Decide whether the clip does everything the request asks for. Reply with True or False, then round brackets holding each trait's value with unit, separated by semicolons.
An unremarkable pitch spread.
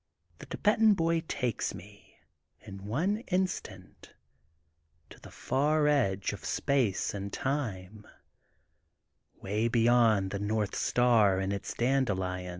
False (6.1 semitones)